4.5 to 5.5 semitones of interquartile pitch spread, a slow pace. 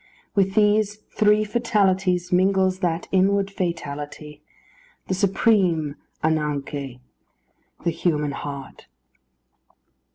Yes: average, 4.8 semitones; slow, 90 wpm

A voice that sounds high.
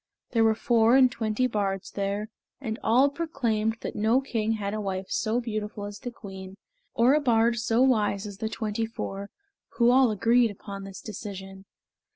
Yes: high, 220 Hz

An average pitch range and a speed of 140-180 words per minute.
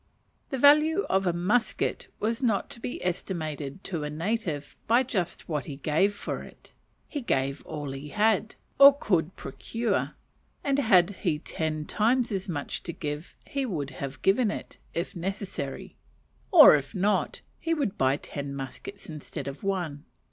No: wide, 7.0 semitones; average, 160 wpm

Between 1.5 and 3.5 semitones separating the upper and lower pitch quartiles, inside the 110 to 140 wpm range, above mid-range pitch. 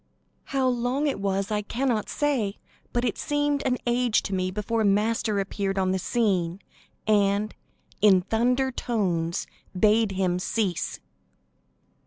No: average, 4.0 semitones; slow, 135 wpm; high, 215 Hz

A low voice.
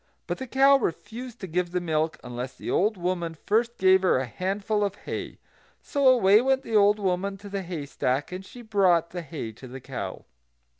No: high, 190 Hz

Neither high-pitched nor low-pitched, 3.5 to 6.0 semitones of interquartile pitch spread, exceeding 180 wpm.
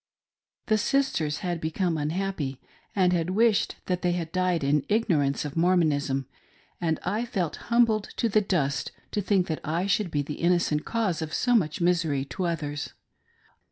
No: medium, 175 Hz; average, 4.5 semitones; average, 160 wpm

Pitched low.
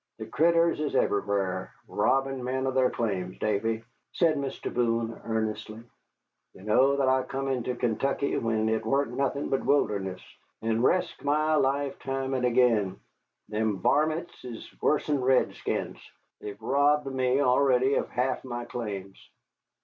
Yes: low, 125 Hz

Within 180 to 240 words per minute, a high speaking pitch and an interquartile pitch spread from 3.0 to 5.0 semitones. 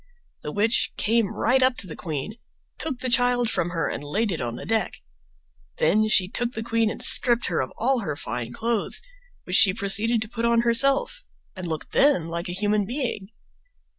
Yes: average, 195 wpm; high, 220 Hz; average, 4.7 semitones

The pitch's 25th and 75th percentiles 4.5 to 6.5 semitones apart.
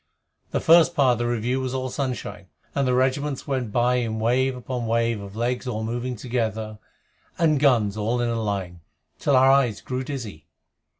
No: average, 2.8 semitones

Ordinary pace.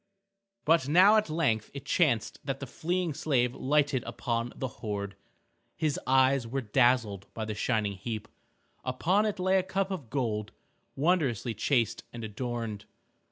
Yes: average, 150 wpm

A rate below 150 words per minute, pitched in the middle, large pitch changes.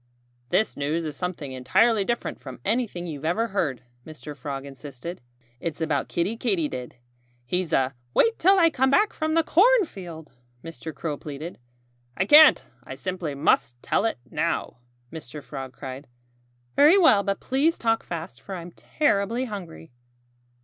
No: average, 155 wpm; medium, 170 Hz; wide, 8.1 semitones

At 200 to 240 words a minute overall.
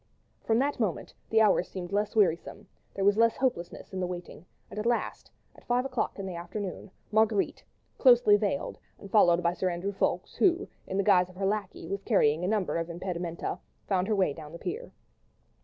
Yes: fast, 205 wpm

